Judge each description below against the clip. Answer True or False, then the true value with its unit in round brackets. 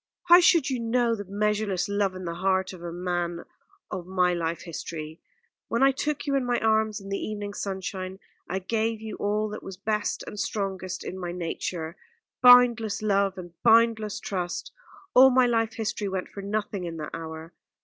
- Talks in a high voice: True (200 Hz)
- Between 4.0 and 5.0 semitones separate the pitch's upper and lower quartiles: False (3.6 semitones)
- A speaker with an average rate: True (185 wpm)